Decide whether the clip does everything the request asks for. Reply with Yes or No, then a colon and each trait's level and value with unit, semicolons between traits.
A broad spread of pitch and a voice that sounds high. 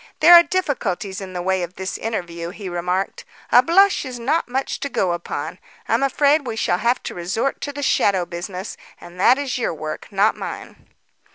Yes: wide, 7.2 semitones; high, 205 Hz